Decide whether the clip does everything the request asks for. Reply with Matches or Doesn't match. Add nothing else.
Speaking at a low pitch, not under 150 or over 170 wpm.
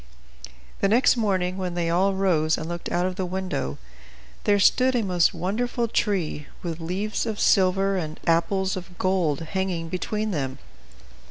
Doesn't match